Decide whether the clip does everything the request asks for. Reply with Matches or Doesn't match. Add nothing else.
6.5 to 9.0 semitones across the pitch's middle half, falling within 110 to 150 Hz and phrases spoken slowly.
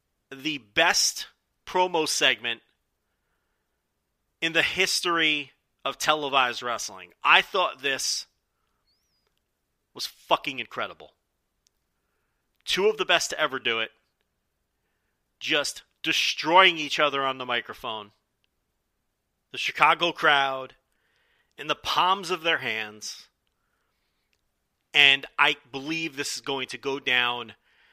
Matches